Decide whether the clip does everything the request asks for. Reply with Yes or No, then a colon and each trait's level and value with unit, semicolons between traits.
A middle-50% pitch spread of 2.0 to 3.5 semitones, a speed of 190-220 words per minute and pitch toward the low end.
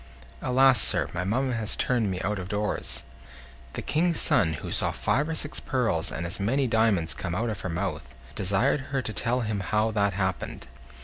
No: average, 5.1 semitones; average, 195 wpm; low, 105 Hz